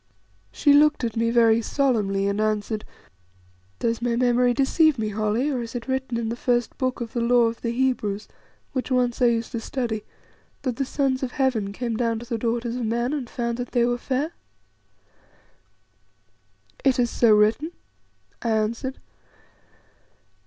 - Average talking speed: Yes, average, 170 wpm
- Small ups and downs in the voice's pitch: Yes, narrow, 2.2 semitones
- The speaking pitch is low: No, high, 240 Hz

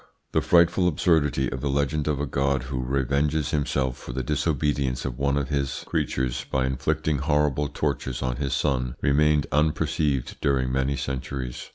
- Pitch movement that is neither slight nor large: No, narrow, 2.2 semitones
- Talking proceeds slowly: No, average, 165 wpm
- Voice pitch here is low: Yes, very low, 70 Hz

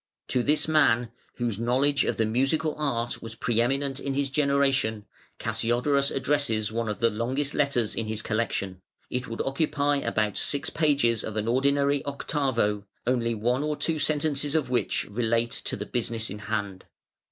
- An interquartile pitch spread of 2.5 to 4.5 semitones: Yes, average, 3.9 semitones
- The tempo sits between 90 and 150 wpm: No, average, 165 wpm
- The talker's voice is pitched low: Yes, low, 125 Hz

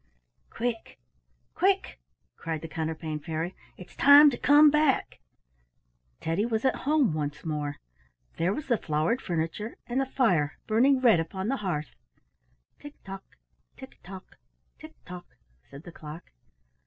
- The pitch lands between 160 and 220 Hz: Yes, high, 190 Hz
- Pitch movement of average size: No, wide, 8.4 semitones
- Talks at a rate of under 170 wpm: Yes, average, 140 wpm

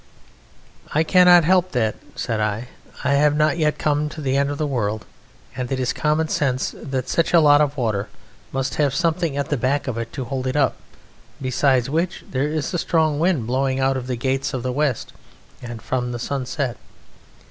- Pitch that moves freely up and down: No, average, 3.1 semitones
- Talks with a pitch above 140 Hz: No, low, 135 Hz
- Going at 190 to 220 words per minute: Yes, average, 200 wpm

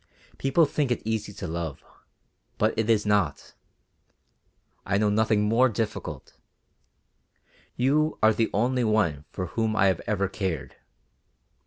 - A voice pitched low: Yes, low, 110 Hz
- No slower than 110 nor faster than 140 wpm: Yes, slow, 135 wpm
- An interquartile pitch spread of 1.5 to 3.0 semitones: Yes, average, 2.7 semitones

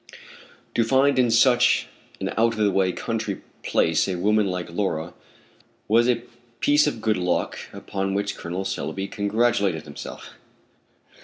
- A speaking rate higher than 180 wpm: No, average, 145 wpm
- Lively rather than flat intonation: No, average, 4.2 semitones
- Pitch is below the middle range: Yes, low, 100 Hz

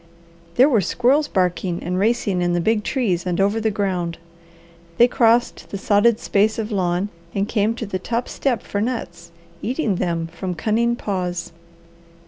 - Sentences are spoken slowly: No, average, 165 wpm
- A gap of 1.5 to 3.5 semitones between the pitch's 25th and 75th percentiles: No, average, 4.5 semitones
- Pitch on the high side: Yes, high, 205 Hz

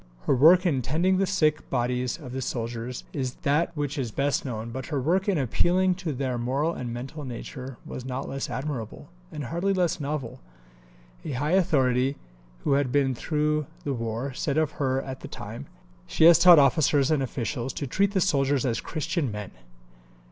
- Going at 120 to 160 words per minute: No, average, 185 wpm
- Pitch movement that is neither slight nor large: Yes, average, 3.9 semitones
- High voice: No, medium, 140 Hz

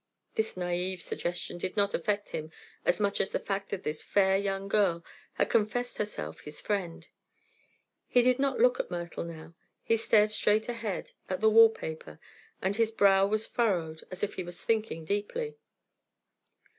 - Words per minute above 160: Yes, average, 170 wpm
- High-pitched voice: Yes, high, 200 Hz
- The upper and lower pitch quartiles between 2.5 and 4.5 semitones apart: Yes, average, 3.8 semitones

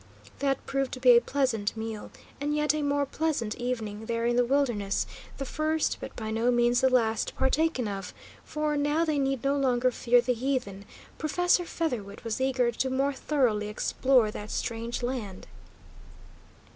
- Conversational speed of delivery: Yes, average, 170 wpm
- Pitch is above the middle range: Yes, very high, 250 Hz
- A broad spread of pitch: No, average, 3.8 semitones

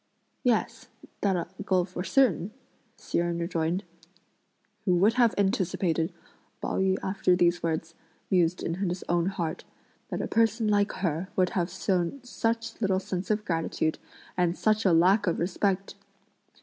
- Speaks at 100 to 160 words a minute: Yes, average, 150 wpm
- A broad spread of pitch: No, average, 2.9 semitones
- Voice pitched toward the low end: No, medium, 185 Hz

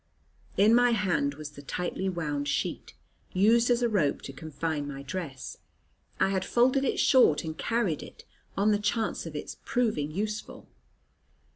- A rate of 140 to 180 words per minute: Yes, average, 160 wpm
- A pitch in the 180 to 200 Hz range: Yes, medium, 185 Hz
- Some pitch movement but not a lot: No, wide, 7.1 semitones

